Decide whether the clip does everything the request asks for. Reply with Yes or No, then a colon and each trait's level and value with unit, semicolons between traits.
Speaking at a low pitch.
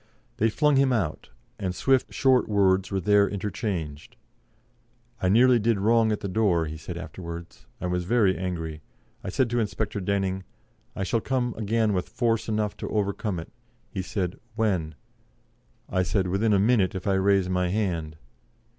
Yes: low, 100 Hz